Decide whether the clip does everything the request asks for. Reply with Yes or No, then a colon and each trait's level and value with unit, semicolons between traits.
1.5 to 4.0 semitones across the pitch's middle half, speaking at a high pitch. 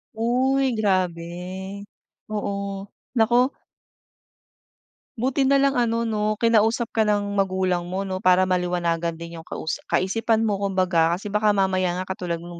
Yes: average, 3.7 semitones; high, 195 Hz